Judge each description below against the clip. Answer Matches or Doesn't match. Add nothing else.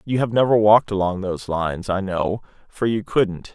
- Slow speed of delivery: Doesn't match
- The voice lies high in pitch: Doesn't match